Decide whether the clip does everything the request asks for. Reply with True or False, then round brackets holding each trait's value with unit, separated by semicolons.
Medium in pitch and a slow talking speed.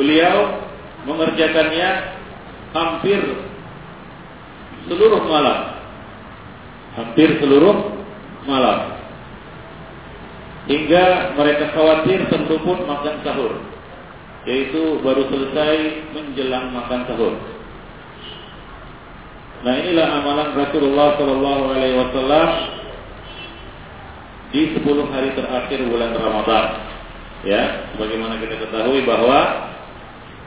True (145 Hz; 75 wpm)